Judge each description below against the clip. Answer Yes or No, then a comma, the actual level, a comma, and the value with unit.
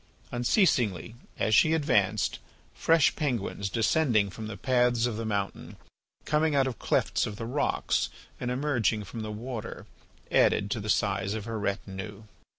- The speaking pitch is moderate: No, low, 115 Hz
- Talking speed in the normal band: Yes, average, 155 wpm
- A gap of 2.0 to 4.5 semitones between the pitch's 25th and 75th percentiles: Yes, average, 3.9 semitones